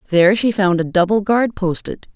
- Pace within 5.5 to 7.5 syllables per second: No, 5.3 syllables/s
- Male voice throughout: No, female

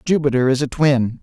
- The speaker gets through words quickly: No, average, 195 wpm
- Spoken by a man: Yes, male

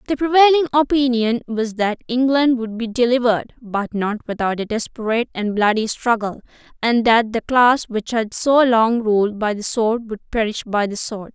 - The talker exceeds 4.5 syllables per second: Yes, 4.7 syllables/s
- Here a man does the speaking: No, female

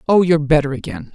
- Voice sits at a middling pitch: Yes, medium, 150 Hz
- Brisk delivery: Yes, fast, 210 wpm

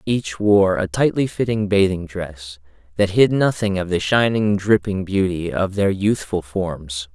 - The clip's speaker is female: No, male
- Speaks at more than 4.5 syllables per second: No, 4.1 syllables/s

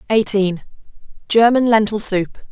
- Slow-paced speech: Yes, slow, 70 wpm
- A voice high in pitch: Yes, high, 210 Hz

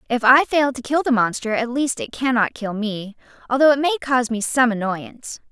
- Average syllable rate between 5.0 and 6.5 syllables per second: Yes, 5.5 syllables/s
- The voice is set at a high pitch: Yes, high, 245 Hz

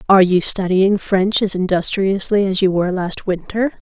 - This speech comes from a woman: Yes, female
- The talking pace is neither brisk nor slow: Yes, average, 170 wpm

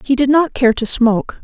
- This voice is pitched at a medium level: No, very high, 255 Hz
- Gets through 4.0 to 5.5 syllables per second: Yes, 5.4 syllables/s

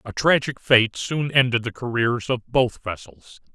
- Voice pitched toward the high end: No, low, 120 Hz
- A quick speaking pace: No, average, 170 wpm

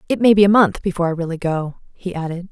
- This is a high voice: No, medium, 180 Hz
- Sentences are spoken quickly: Yes, fast, 265 wpm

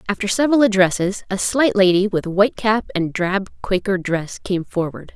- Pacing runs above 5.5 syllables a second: No, 5.1 syllables/s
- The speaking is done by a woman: Yes, female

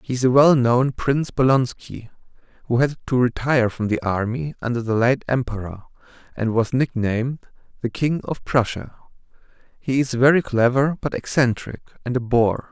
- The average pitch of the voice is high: No, low, 125 Hz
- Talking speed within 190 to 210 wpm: No, average, 155 wpm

